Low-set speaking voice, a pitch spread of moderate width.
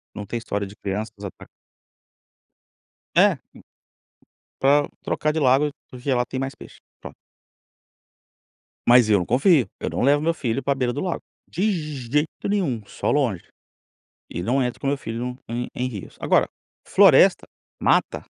Yes: low, 125 Hz; average, 4.0 semitones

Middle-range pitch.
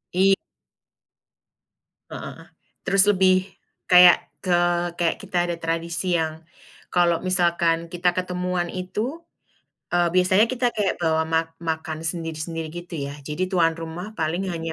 Yes: medium, 175 Hz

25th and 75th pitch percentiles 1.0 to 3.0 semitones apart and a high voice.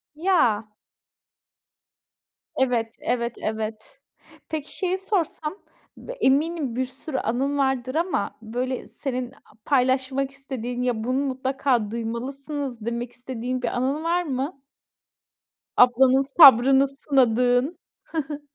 Yes: average, 2.7 semitones; very high, 260 Hz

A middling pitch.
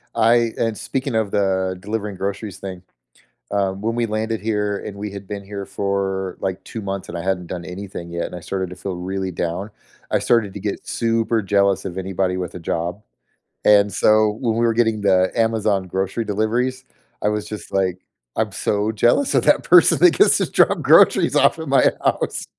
No: low, 100 Hz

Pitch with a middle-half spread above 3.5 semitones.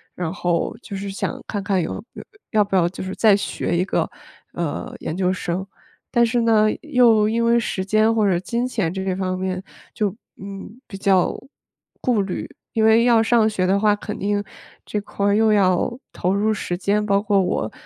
No: average, 2.8 semitones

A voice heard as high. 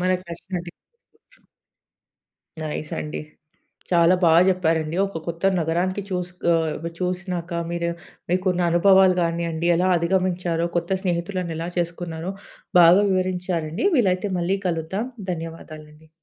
No: medium, 175 Hz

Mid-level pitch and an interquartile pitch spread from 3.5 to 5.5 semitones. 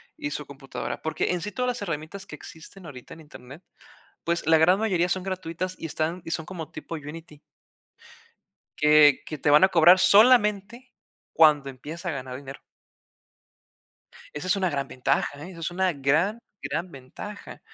Yes: medium, 165 Hz; average, 4.0 semitones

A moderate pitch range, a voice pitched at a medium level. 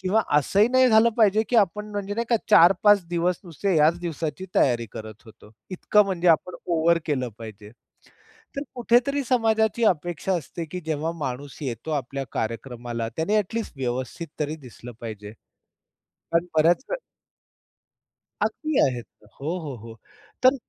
No: wide, 7.7 semitones; medium, 170 Hz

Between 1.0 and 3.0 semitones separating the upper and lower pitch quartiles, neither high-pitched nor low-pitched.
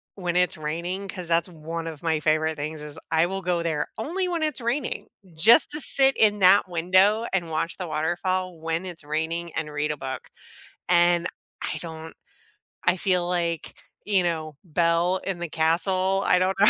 Yes: average, 2.7 semitones; medium, 175 Hz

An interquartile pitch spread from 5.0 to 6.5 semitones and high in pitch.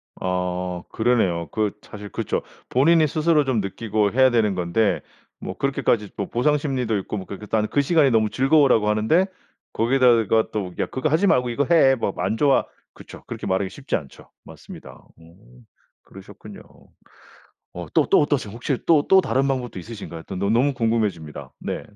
No: wide, 5.5 semitones; low, 115 Hz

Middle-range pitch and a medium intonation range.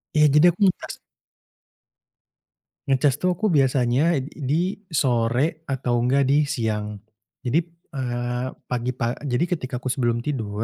No: low, 130 Hz; average, 3.8 semitones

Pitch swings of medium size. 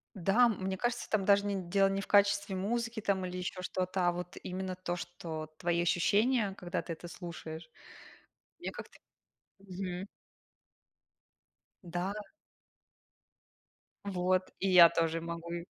No: narrow, 2.3 semitones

